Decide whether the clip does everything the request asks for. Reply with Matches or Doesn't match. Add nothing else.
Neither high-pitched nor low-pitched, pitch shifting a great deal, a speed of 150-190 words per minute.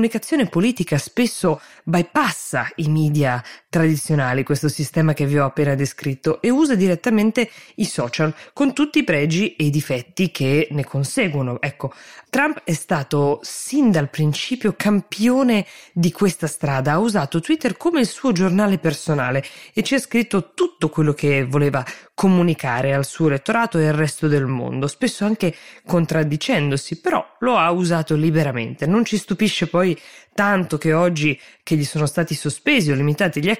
Matches